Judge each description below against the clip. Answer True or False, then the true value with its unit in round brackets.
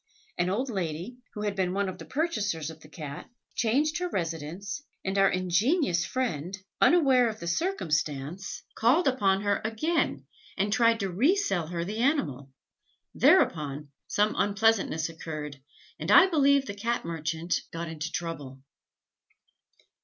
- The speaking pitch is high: True (195 Hz)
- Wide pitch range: True (6.5 semitones)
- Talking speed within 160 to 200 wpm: False (145 wpm)